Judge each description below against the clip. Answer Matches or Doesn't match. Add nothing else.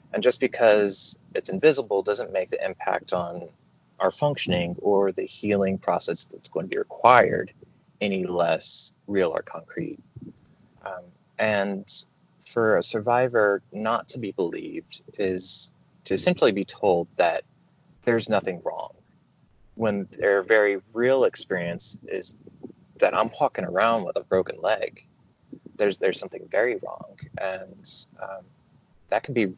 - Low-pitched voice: Matches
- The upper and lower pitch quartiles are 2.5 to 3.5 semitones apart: Doesn't match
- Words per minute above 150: Doesn't match